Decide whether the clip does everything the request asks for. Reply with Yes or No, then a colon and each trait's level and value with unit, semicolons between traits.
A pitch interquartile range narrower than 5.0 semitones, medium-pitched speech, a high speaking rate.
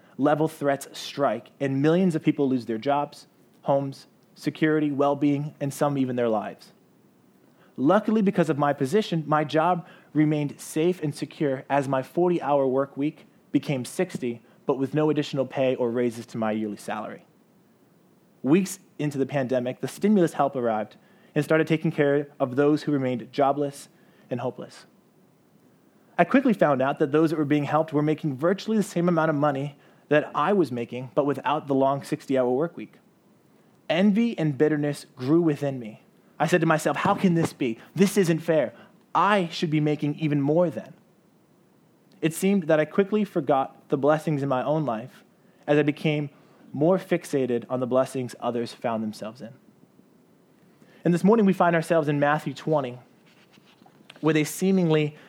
No: average, 3.7 semitones; medium, 150 Hz; average, 170 wpm